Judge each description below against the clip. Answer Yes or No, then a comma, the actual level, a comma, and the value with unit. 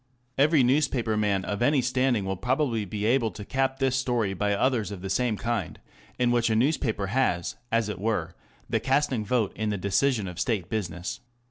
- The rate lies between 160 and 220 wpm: Yes, average, 195 wpm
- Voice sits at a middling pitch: No, low, 115 Hz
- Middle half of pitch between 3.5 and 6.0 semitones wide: Yes, average, 4.1 semitones